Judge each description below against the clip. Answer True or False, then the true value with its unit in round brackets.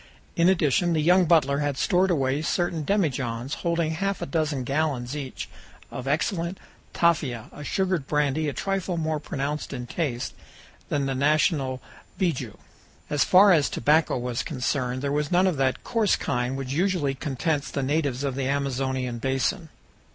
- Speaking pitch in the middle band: True (145 Hz)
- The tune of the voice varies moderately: True (4.0 semitones)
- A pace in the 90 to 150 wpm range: False (160 wpm)